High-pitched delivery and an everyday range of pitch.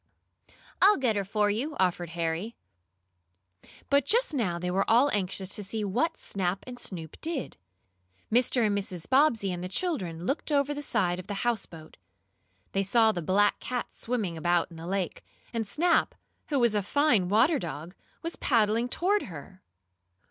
No: high, 210 Hz; wide, 6.2 semitones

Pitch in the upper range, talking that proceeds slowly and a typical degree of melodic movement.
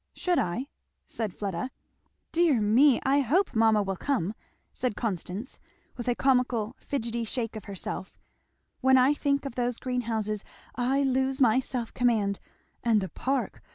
No: high, 245 Hz; average, 150 wpm; average, 3.6 semitones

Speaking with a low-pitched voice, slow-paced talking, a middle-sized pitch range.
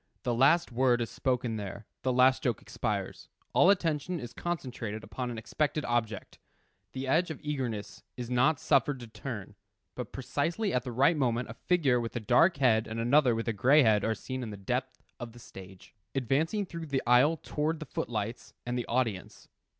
No: low, 125 Hz; average, 195 wpm; average, 4.1 semitones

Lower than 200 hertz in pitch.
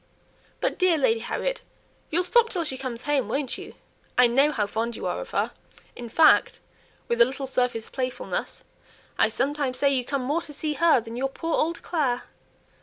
No: very high, 270 Hz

